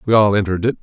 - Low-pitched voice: Yes, low, 105 Hz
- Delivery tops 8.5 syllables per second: Yes, 8.8 syllables/s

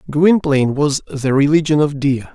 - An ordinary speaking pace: Yes, average, 155 wpm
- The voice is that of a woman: No, male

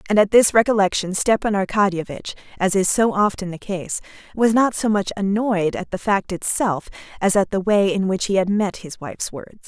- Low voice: No, high, 200 Hz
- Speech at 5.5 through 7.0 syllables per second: No, 5.2 syllables/s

